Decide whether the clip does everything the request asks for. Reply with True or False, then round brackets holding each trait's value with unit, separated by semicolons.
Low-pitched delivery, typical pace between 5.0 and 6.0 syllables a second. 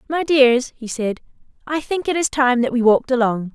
False (255 Hz; 5.3 syllables/s)